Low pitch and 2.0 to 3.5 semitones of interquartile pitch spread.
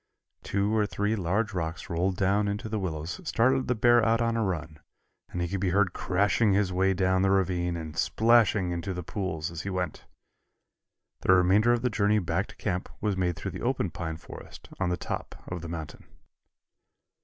Yes: very low, 95 Hz; average, 3.1 semitones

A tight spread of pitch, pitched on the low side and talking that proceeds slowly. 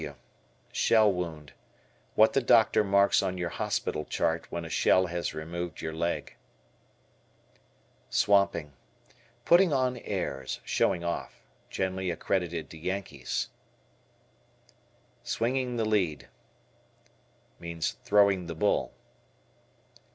No: average, 3.8 semitones; very low, 90 Hz; slow, 100 wpm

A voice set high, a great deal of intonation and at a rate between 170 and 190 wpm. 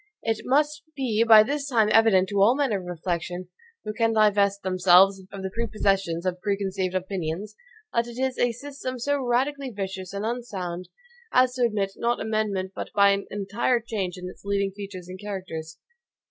No: high, 205 Hz; average, 3.8 semitones; average, 180 wpm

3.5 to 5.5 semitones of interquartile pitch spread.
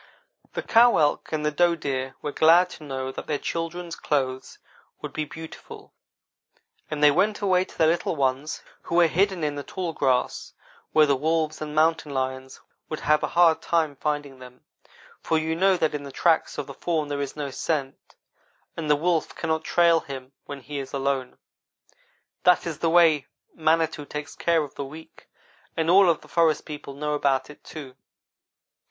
No: average, 2.8 semitones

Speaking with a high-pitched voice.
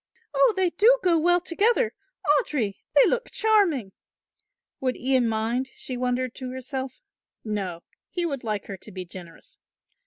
Yes: very high, 260 Hz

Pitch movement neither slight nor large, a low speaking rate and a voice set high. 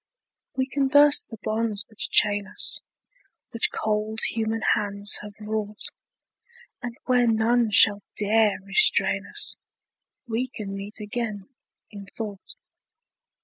No: narrow, 2.1 semitones; slow, 120 wpm; high, 220 Hz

